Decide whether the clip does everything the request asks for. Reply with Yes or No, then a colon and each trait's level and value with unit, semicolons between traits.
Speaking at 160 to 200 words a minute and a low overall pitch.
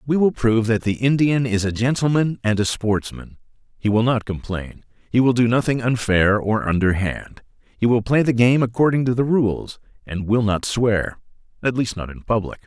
Yes: average, 190 wpm; low, 115 Hz